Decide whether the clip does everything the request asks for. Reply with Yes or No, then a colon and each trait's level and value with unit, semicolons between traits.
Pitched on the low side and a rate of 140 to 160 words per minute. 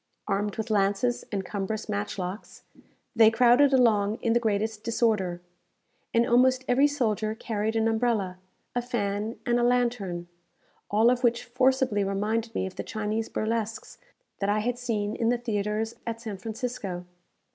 No: high, 220 Hz; average, 155 wpm